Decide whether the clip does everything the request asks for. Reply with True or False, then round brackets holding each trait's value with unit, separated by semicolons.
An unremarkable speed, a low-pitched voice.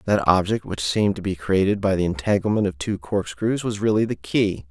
False (215 wpm; 95 Hz)